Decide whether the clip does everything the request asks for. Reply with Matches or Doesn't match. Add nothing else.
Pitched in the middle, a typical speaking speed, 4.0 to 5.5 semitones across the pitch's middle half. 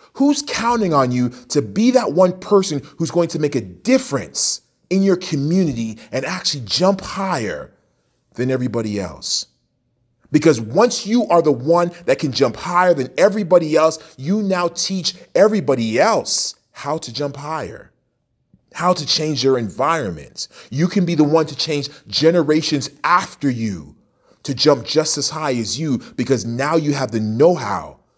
Matches